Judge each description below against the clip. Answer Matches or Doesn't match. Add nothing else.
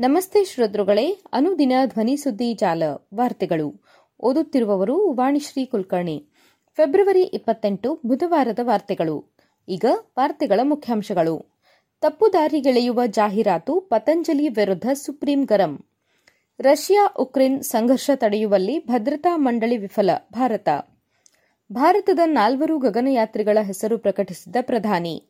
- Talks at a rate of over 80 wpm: Matches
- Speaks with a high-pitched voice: Matches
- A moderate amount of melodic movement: Doesn't match